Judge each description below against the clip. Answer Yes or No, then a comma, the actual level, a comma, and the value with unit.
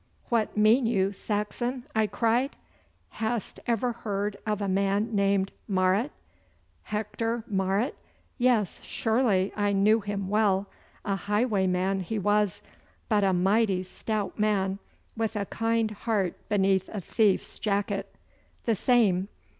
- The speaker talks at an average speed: No, slow, 125 wpm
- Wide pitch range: No, narrow, 2.4 semitones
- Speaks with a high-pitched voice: Yes, high, 210 Hz